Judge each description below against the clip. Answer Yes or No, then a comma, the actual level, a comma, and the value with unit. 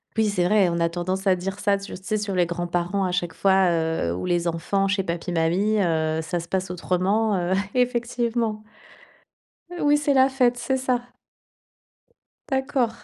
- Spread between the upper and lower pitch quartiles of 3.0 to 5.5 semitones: Yes, average, 4.5 semitones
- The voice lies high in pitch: Yes, high, 195 Hz